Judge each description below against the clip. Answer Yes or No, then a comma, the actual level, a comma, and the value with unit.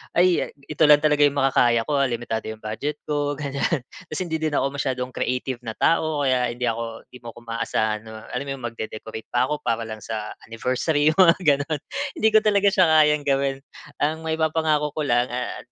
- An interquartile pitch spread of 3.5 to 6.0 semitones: Yes, average, 4.4 semitones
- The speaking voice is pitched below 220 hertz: Yes, medium, 140 Hz